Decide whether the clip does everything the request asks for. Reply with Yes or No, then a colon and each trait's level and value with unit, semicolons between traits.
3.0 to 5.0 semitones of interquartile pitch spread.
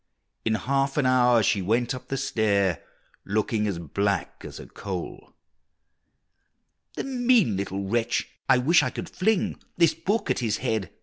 No: wide, 5.4 semitones